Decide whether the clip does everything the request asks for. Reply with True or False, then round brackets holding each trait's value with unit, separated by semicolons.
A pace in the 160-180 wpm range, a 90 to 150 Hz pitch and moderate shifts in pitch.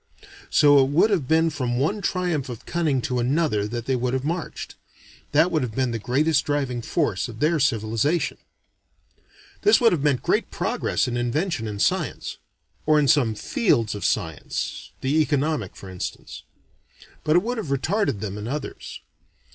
True (170 wpm; 140 Hz; 5.0 semitones)